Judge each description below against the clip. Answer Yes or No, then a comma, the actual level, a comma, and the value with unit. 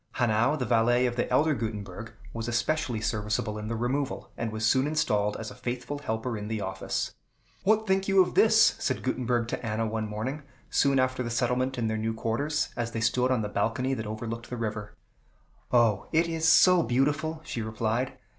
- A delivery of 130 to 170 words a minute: No, average, 195 wpm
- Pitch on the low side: Yes, low, 120 Hz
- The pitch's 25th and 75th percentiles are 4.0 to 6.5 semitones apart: No, average, 3.3 semitones